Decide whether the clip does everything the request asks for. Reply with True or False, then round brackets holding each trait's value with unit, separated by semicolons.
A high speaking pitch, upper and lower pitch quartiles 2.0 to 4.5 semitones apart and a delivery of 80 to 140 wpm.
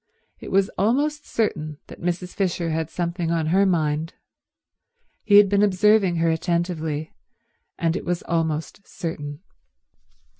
False (170 Hz; 3.4 semitones; 135 wpm)